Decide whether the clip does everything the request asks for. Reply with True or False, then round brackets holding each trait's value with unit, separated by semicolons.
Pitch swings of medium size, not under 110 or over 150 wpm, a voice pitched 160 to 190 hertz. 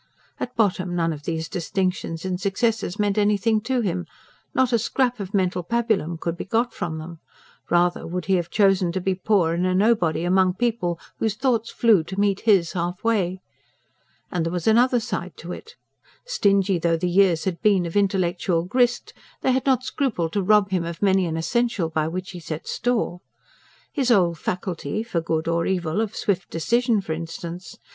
False (4.3 semitones; 190 wpm; 185 Hz)